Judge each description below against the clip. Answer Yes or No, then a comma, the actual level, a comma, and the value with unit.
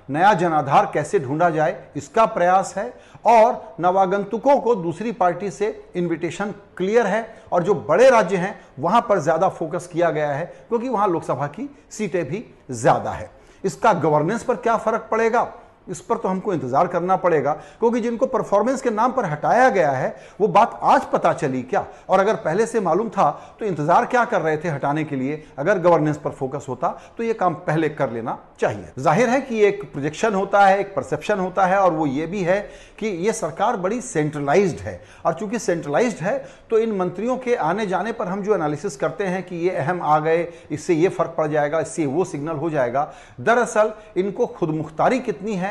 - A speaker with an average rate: No, fast, 195 wpm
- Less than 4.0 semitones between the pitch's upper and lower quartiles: No, average, 5.2 semitones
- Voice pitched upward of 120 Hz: Yes, high, 190 Hz